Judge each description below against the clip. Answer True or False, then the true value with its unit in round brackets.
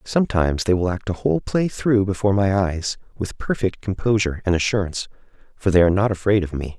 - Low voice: True (95 Hz)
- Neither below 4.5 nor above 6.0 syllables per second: False (6.4 syllables/s)